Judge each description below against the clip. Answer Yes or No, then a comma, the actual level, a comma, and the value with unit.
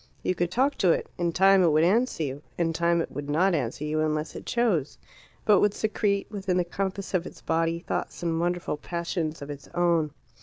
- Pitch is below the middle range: No, medium, 170 Hz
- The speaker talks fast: Yes, fast, 215 wpm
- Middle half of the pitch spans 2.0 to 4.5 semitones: Yes, average, 3.5 semitones